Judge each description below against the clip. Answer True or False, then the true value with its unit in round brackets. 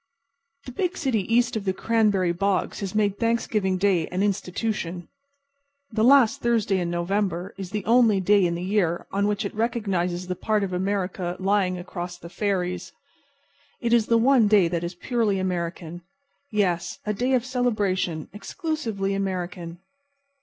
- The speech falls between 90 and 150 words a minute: False (160 wpm)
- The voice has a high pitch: True (195 Hz)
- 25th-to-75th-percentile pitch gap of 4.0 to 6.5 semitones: False (3.5 semitones)